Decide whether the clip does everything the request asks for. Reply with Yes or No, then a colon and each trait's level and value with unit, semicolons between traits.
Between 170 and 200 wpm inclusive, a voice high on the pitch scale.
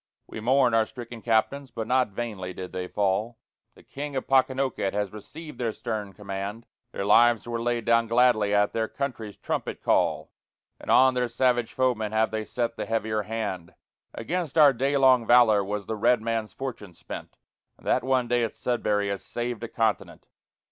No: average, 185 wpm; low, 115 Hz